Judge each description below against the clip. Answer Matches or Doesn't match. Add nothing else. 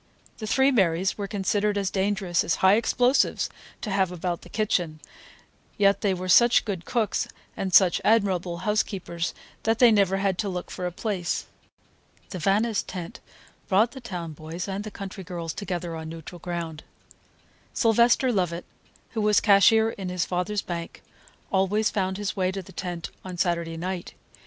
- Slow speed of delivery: Doesn't match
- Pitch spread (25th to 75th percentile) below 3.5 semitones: Matches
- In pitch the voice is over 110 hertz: Matches